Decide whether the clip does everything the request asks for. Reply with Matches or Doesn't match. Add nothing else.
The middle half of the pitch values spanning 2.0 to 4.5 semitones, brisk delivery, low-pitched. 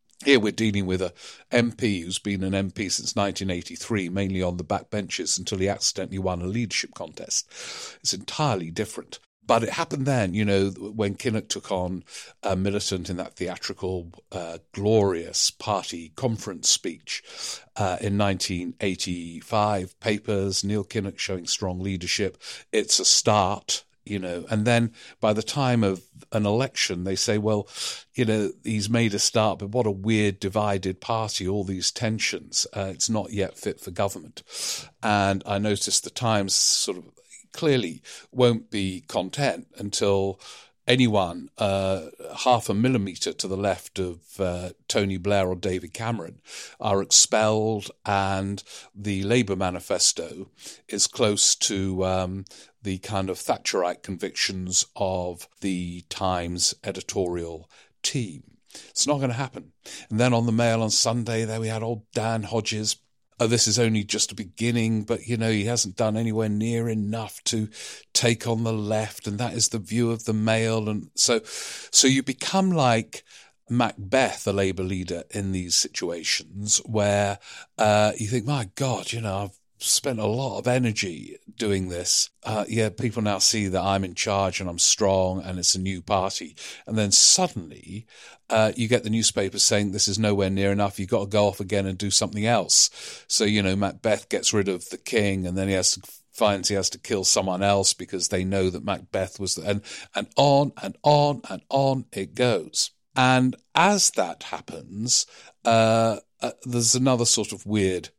Doesn't match